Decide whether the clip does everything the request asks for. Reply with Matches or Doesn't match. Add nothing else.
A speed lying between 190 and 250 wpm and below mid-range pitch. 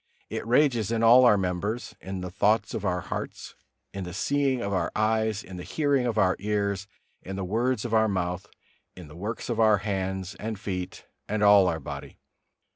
Matches